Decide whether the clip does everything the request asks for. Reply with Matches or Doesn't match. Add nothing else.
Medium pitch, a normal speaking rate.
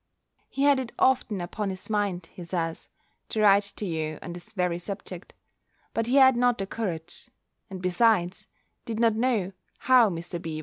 Doesn't match